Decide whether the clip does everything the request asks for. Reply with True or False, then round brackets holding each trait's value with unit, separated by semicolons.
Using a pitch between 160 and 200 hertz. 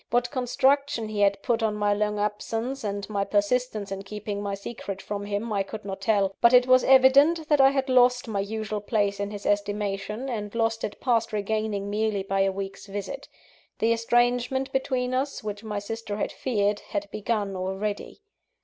False (215 Hz)